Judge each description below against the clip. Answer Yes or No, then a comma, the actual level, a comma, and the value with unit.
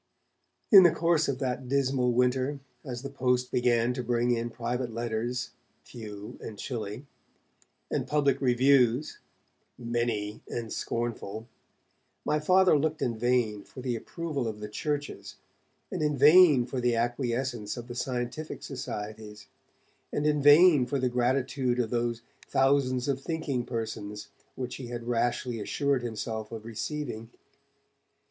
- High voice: No, low, 125 Hz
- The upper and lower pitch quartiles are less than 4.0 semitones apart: Yes, average, 2.9 semitones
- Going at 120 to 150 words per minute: Yes, average, 140 wpm